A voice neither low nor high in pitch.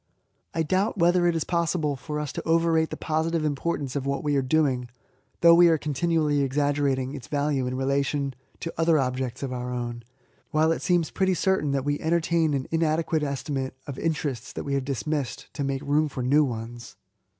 Yes: medium, 145 Hz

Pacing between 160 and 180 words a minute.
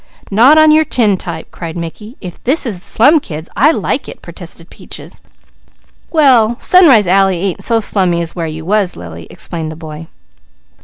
Yes: average, 170 wpm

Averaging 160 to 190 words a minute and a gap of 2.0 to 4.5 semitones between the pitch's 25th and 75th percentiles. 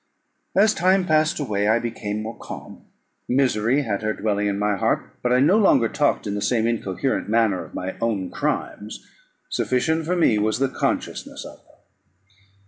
No: average, 175 wpm; wide, 5.4 semitones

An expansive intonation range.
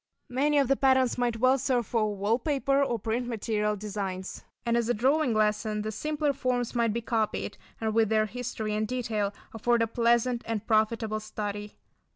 No: narrow, 2.6 semitones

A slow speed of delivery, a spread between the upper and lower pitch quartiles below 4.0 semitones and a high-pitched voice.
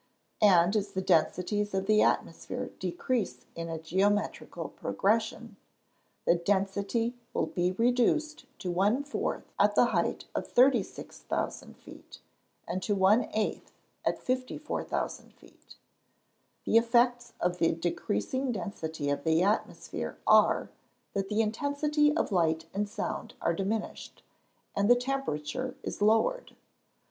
No: slow, 125 wpm; average, 5.3 semitones; high, 205 Hz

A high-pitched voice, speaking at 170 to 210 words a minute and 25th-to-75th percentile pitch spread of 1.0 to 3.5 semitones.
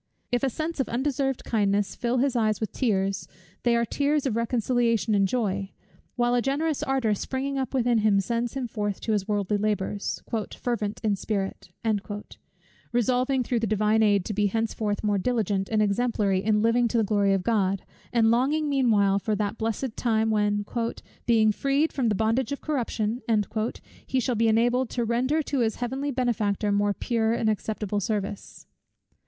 Yes: high, 225 Hz; average, 175 wpm; average, 3.2 semitones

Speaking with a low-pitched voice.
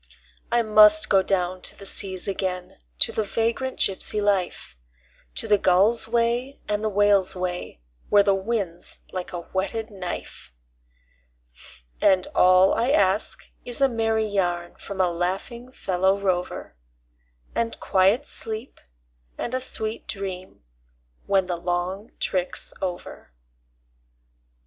No: high, 195 Hz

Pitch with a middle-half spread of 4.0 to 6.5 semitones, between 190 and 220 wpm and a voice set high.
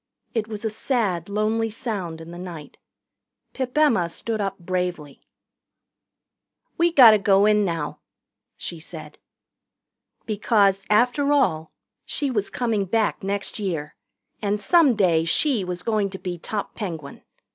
No: average, 4.3 semitones; slow, 135 wpm; high, 200 Hz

